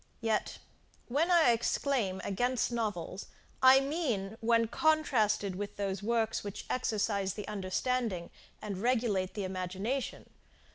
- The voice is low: No, high, 220 Hz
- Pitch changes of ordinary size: Yes, average, 4.3 semitones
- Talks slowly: Yes, slow, 115 wpm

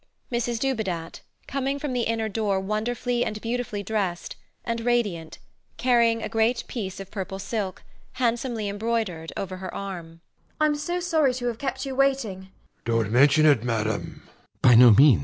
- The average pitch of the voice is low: No, high, 230 Hz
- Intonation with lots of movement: No, average, 4.1 semitones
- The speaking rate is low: Yes, slow, 130 wpm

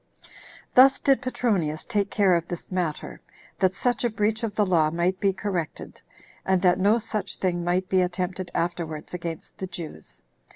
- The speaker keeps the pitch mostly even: No, average, 3.2 semitones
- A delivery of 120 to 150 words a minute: No, average, 175 wpm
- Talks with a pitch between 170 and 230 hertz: Yes, medium, 185 Hz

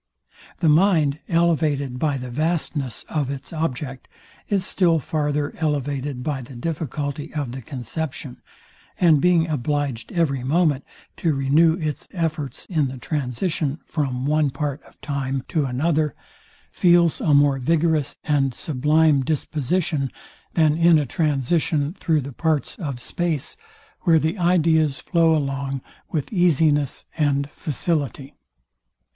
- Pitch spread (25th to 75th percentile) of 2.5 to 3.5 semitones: Yes, average, 2.9 semitones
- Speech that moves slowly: Yes, slow, 130 wpm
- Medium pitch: Yes, medium, 150 Hz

